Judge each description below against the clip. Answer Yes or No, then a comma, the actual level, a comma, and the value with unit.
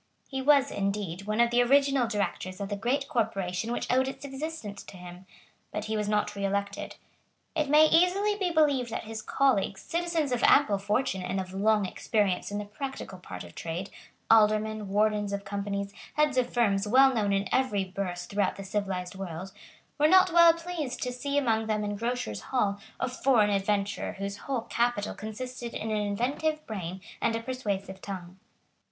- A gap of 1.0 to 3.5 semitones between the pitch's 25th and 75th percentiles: No, average, 4.9 semitones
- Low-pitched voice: No, high, 215 Hz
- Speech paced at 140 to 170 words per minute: No, average, 180 wpm